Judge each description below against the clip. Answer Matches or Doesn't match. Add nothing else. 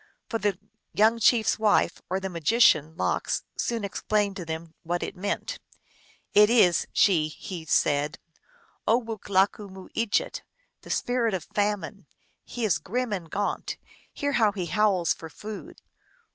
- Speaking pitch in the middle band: Doesn't match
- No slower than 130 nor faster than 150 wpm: Matches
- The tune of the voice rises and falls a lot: Doesn't match